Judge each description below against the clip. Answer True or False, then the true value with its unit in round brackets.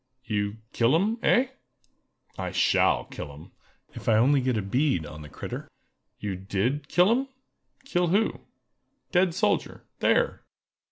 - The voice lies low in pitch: True (130 Hz)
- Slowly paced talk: True (130 wpm)